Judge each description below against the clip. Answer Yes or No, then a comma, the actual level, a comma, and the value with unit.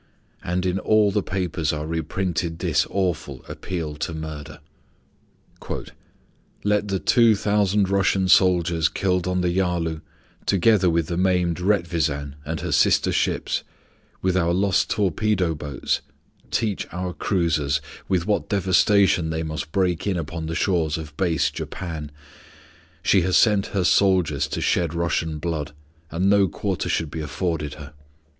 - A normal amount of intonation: Yes, average, 3.1 semitones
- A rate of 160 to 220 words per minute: No, average, 145 wpm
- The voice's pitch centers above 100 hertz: No, very low, 90 Hz